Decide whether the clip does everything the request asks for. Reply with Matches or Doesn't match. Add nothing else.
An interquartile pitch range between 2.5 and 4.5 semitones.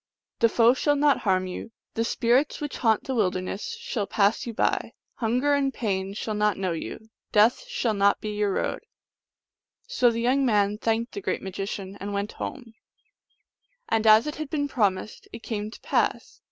Matches